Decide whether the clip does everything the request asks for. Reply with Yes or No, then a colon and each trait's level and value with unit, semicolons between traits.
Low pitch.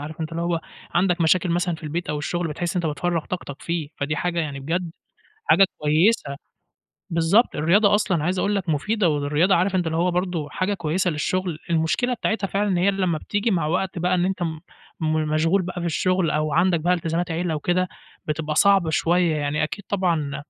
No: medium, 170 Hz